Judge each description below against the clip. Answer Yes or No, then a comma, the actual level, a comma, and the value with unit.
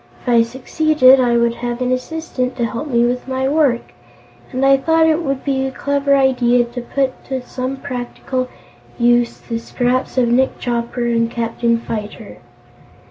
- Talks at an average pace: Yes, average, 170 wpm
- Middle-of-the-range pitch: No, very high, 255 Hz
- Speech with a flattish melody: Yes, narrow, 2.2 semitones